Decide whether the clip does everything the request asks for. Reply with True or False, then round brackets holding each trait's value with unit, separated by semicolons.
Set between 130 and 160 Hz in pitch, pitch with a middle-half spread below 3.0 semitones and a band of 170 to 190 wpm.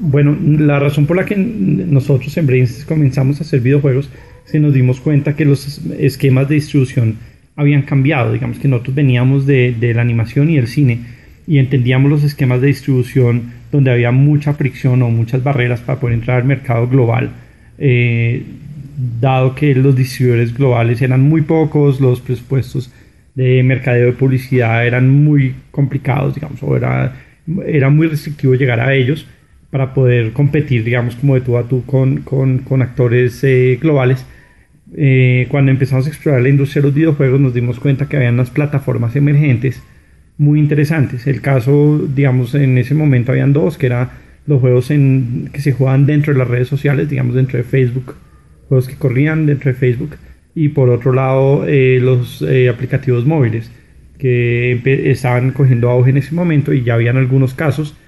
True (135 Hz; 2.4 semitones; 175 wpm)